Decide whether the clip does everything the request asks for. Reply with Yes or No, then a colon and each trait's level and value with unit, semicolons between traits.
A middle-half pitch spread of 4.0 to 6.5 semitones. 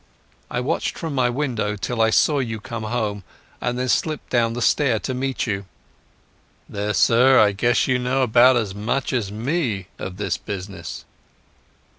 No: average, 3.6 semitones